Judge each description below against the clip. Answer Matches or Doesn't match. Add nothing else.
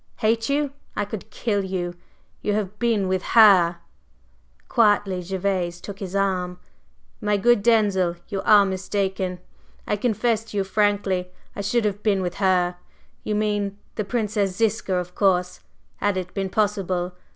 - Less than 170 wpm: Matches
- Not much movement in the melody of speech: Matches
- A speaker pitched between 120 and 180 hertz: Doesn't match